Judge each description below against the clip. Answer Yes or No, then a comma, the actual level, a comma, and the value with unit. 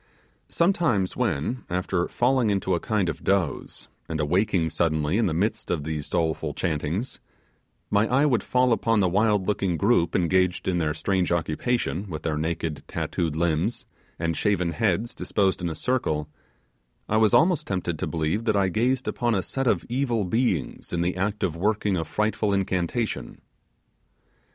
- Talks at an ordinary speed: Yes, average, 170 wpm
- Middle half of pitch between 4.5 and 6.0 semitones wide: Yes, average, 4.9 semitones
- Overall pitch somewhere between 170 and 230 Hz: No, very low, 95 Hz